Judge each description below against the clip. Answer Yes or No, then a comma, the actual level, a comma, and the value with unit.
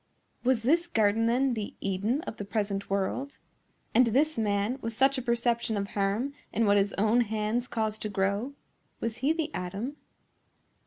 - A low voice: No, high, 225 Hz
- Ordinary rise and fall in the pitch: Yes, average, 3.9 semitones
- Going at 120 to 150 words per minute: No, average, 165 wpm